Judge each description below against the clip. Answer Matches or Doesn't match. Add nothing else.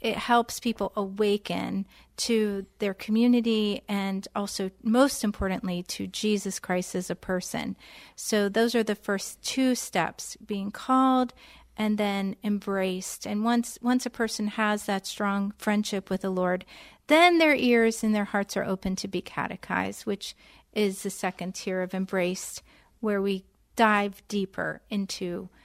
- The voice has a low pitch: Doesn't match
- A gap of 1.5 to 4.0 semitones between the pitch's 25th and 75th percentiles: Matches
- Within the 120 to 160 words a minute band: Matches